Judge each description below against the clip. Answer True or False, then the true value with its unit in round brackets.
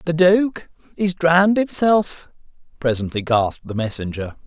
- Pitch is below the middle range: False (160 Hz)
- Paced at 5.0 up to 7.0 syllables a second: False (4.6 syllables/s)